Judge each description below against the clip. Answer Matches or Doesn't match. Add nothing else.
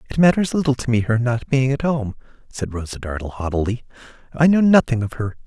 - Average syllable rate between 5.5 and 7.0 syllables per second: Matches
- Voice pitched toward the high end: Doesn't match